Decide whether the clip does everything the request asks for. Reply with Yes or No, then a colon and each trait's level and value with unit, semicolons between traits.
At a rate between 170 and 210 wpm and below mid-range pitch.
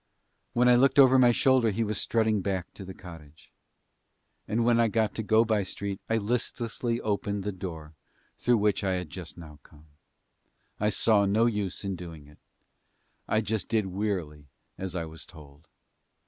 Yes: average, 175 wpm; low, 100 Hz